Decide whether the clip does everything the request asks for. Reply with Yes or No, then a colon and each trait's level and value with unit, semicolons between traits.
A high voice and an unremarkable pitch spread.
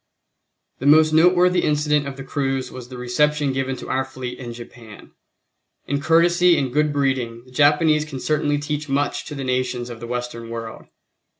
No: low, 135 Hz; average, 3.3 semitones